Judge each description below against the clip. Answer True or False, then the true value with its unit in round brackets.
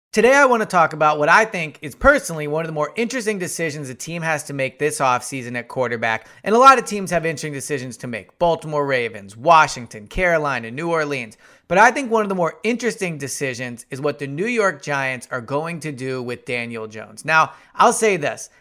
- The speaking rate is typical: False (220 wpm)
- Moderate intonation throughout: False (5.7 semitones)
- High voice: False (150 Hz)